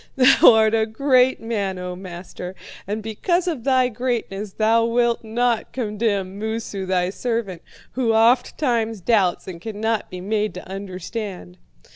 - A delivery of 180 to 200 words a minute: No, average, 140 wpm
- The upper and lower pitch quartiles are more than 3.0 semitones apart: Yes, average, 3.5 semitones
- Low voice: No, high, 220 Hz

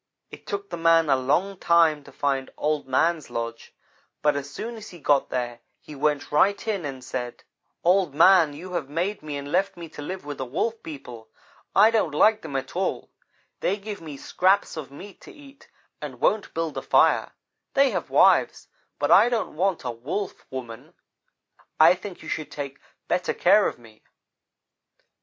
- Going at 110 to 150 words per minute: No, average, 185 wpm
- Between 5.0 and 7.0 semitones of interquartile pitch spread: Yes, wide, 5.6 semitones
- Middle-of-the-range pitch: Yes, medium, 160 Hz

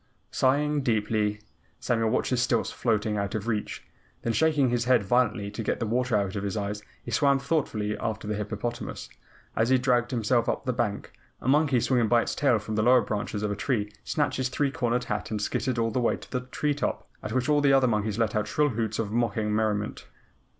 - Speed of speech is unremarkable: No, fast, 225 wpm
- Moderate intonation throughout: Yes, average, 3.2 semitones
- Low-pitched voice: Yes, low, 115 Hz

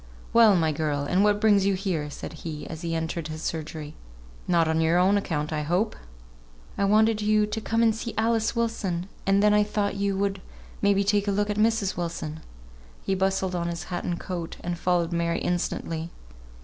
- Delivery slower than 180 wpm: No, average, 200 wpm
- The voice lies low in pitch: No, medium, 185 Hz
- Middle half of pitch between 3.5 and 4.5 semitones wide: Yes, average, 3.9 semitones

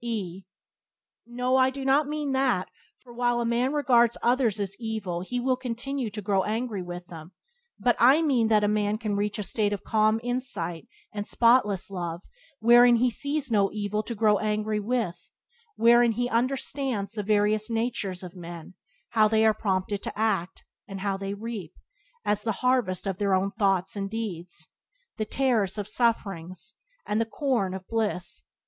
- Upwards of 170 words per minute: Yes, average, 180 wpm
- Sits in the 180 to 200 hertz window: No, high, 215 Hz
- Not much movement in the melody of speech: No, average, 3.6 semitones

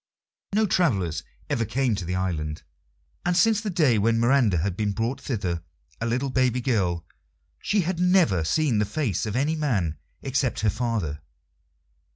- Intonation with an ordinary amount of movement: No, wide, 7.2 semitones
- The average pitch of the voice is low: Yes, low, 115 Hz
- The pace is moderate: Yes, average, 165 wpm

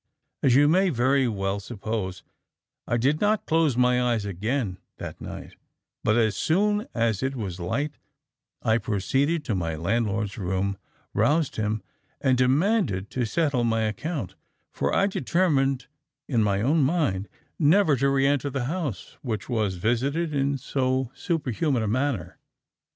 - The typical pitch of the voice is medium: No, low, 125 Hz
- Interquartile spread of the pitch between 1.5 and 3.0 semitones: No, wide, 5.4 semitones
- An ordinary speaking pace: Yes, average, 145 wpm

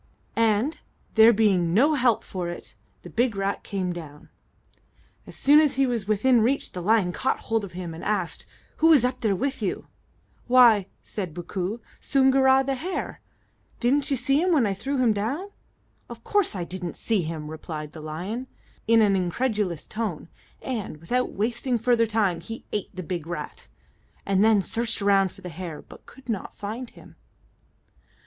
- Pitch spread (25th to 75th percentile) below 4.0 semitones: No, wide, 5.5 semitones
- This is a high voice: Yes, high, 215 Hz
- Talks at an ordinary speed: Yes, average, 175 wpm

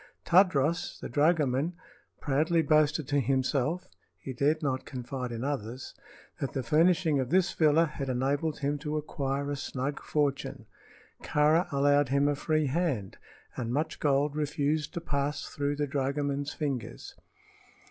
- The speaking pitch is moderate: Yes, medium, 145 Hz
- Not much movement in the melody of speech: Yes, narrow, 2.1 semitones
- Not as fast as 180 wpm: Yes, average, 145 wpm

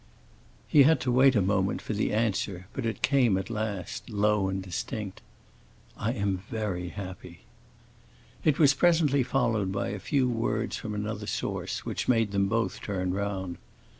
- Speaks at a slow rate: No, average, 165 wpm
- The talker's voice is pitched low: Yes, low, 105 Hz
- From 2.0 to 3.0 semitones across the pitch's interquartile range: No, average, 3.9 semitones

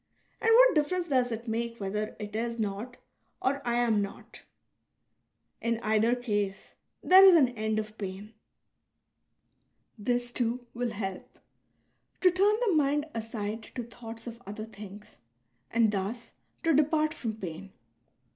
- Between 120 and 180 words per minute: Yes, average, 145 wpm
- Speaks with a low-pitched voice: No, high, 230 Hz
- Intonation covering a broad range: No, average, 3.4 semitones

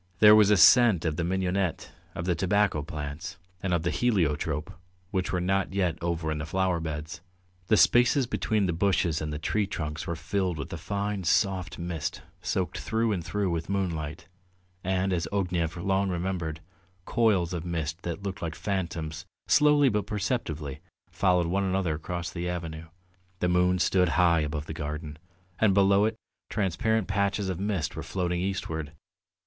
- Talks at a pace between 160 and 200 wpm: Yes, average, 170 wpm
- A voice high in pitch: No, very low, 90 Hz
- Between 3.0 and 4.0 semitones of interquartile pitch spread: Yes, average, 3.3 semitones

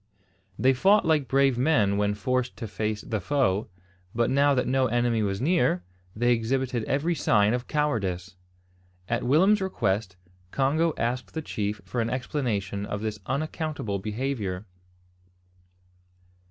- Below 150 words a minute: Yes, average, 140 wpm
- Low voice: Yes, low, 120 Hz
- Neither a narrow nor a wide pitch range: Yes, average, 5.0 semitones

